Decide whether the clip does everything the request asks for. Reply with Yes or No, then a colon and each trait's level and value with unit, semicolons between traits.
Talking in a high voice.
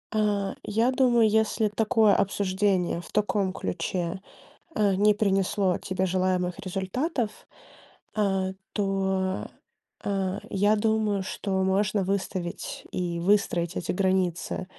Yes: high, 195 Hz